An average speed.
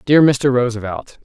Yes: average, 145 wpm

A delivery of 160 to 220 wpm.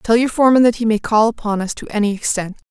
No: fast, 265 wpm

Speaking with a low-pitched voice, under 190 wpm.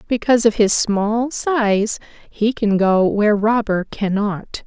No: high, 215 Hz; average, 140 wpm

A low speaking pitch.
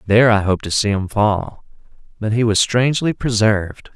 Yes: low, 110 Hz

